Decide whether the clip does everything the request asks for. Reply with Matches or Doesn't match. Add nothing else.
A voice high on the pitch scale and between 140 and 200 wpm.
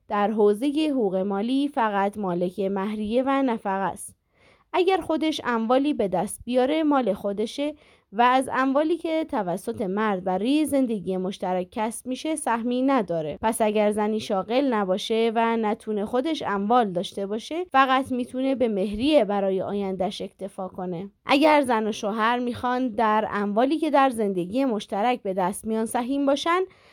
Matches